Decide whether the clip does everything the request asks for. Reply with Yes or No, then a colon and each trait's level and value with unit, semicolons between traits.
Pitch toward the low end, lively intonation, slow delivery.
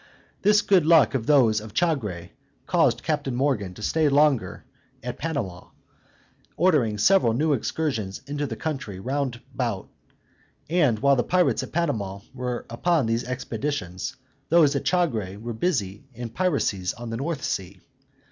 No: low, 130 Hz; wide, 5.9 semitones; average, 145 wpm